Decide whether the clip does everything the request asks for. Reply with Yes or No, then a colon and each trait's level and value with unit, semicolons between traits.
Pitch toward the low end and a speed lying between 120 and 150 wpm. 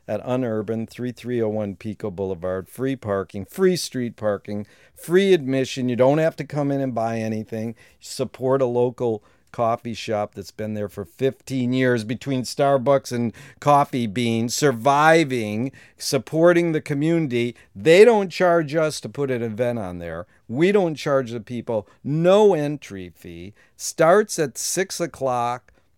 Yes: low, 125 Hz; average, 145 wpm